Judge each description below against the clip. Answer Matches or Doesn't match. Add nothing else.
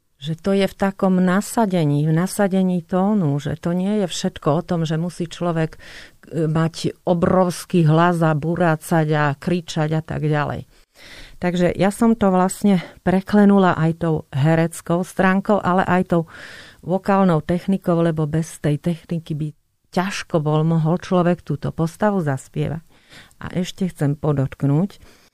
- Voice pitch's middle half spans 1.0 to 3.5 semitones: Matches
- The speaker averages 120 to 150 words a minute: Matches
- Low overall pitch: Doesn't match